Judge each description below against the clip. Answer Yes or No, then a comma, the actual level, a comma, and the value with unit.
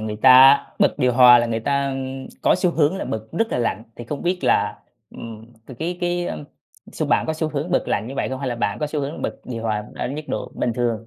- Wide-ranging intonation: No, average, 4.5 semitones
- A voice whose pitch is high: No, low, 130 Hz